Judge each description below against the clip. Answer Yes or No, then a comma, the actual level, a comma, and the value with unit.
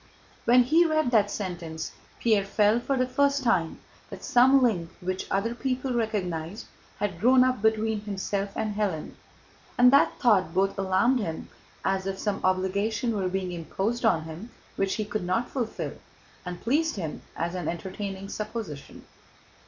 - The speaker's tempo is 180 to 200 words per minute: No, average, 160 wpm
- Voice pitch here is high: Yes, high, 205 Hz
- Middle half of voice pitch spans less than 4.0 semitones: No, average, 4.4 semitones